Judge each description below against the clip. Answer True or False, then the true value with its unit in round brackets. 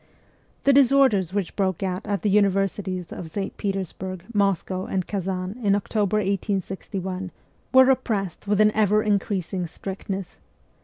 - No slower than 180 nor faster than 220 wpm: False (135 wpm)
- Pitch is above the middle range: True (195 Hz)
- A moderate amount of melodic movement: False (2.0 semitones)